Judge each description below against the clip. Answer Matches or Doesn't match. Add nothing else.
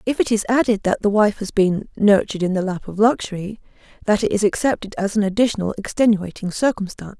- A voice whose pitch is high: Matches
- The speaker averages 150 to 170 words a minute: Doesn't match